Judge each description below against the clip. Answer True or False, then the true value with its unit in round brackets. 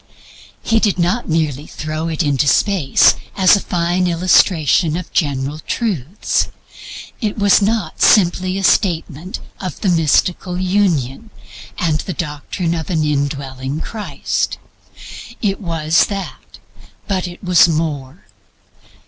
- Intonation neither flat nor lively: True (3.7 semitones)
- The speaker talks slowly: True (125 wpm)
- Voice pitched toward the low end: False (170 Hz)